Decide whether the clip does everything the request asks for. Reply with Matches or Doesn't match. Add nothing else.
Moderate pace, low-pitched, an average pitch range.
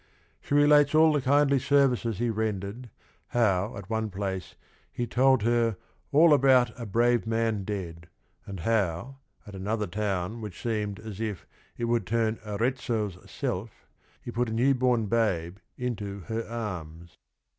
Matches